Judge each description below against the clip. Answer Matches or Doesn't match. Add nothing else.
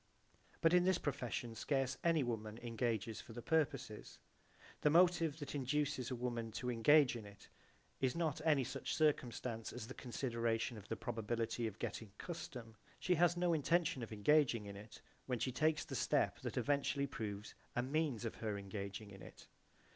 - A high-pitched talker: Doesn't match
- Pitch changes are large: Doesn't match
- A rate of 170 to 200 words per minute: Matches